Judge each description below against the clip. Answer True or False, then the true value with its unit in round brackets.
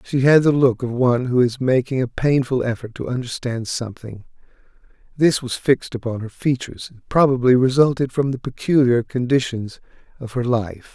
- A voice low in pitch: True (125 Hz)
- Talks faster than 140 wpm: True (170 wpm)